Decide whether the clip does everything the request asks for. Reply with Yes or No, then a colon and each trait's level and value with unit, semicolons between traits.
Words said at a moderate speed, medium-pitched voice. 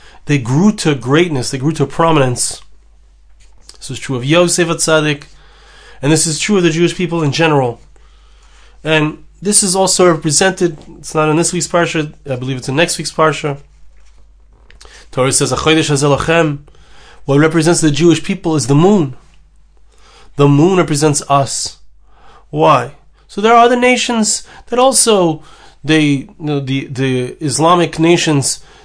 Yes: average, 150 wpm; medium, 155 Hz